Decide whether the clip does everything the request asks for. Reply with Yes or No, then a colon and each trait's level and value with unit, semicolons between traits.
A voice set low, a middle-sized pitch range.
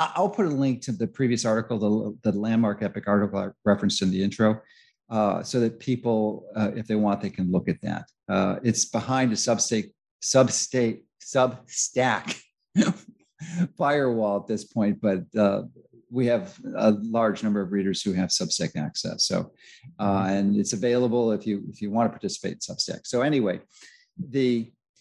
Yes: low, 115 Hz; average, 3.8 semitones